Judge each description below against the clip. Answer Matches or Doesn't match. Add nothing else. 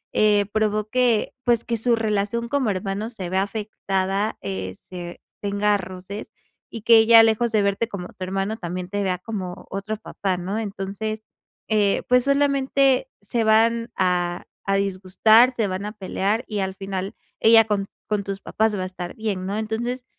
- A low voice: Doesn't match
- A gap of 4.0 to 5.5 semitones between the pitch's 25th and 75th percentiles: Doesn't match